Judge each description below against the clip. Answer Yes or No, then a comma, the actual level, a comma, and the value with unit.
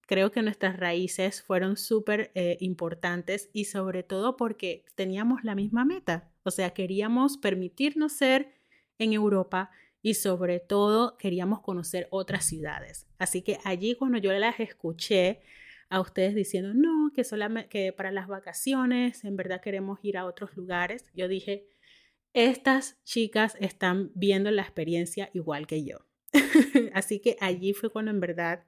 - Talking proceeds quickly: No, average, 150 wpm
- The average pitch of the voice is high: Yes, high, 195 Hz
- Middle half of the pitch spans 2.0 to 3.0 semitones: No, average, 3.4 semitones